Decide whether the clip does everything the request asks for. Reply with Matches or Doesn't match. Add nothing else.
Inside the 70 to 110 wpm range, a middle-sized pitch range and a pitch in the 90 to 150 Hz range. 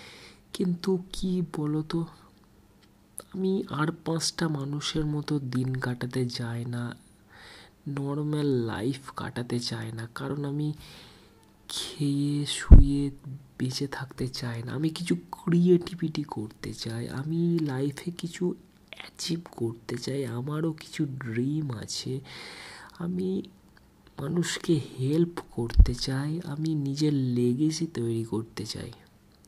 Matches